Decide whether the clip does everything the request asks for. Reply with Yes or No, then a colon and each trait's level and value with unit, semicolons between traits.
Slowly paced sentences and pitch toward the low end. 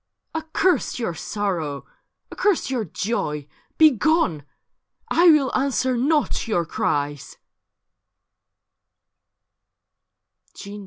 No: slow, 85 wpm; high, 240 Hz